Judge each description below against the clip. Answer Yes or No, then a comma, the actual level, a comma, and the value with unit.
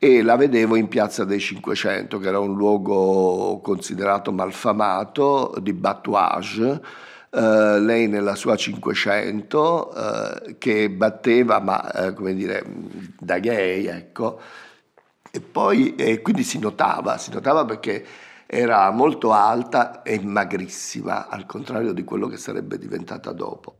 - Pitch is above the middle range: No, low, 100 Hz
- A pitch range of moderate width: No, narrow, 2.1 semitones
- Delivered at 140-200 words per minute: No, average, 130 wpm